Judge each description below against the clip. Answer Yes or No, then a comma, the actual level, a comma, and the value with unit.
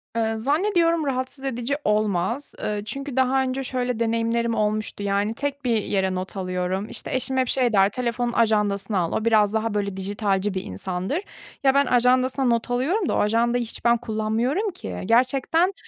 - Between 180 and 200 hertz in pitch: No, high, 230 Hz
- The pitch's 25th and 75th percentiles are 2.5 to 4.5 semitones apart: Yes, average, 4.0 semitones